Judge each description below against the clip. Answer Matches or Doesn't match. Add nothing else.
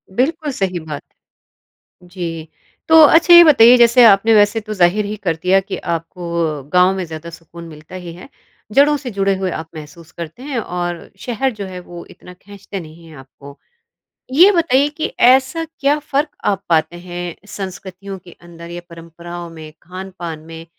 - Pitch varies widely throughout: Matches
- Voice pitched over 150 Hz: Matches